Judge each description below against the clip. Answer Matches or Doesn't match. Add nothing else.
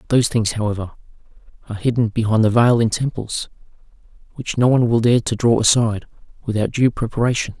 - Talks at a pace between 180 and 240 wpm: Doesn't match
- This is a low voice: Matches